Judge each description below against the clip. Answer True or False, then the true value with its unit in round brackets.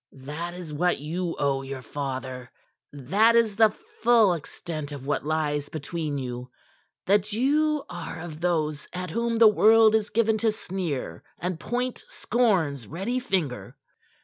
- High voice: False (175 Hz)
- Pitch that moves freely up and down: True (7.0 semitones)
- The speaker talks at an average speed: True (150 wpm)